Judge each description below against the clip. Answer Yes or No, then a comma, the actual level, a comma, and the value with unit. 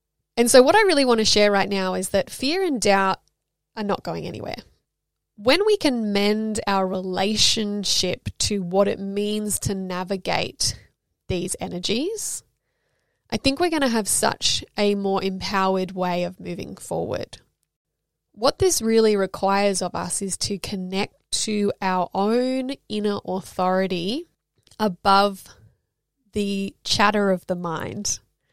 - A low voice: No, high, 200 Hz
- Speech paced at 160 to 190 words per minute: No, average, 140 wpm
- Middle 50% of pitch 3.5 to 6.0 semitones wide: No, average, 2.7 semitones